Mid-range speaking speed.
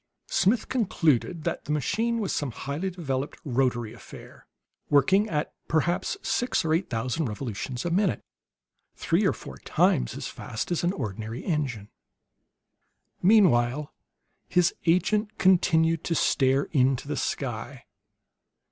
No: slow, 130 wpm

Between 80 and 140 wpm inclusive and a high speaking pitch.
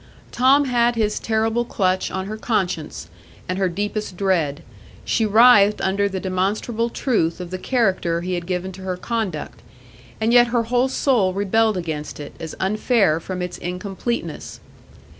No: average, 160 wpm; high, 195 Hz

